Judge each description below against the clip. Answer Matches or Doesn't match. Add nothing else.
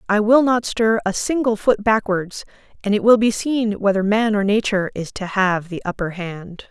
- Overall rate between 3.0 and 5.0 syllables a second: Matches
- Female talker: Matches